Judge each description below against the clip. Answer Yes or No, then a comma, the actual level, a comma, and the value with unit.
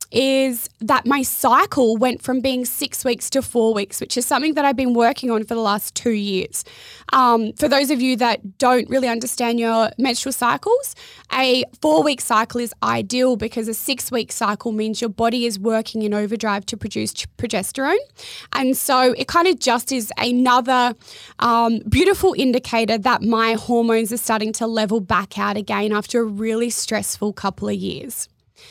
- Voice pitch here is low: No, high, 235 Hz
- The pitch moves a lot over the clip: No, narrow, 2.5 semitones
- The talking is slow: No, average, 180 wpm